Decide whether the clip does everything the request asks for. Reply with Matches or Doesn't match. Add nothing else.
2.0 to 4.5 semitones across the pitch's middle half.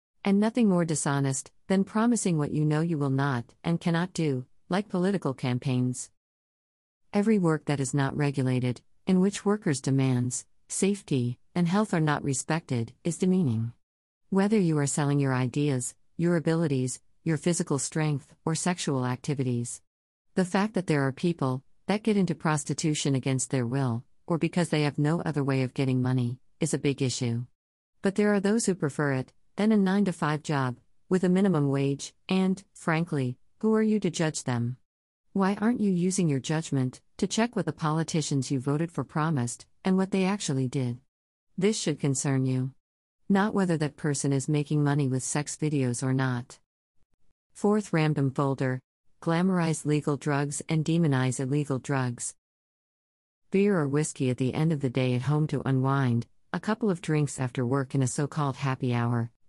Doesn't match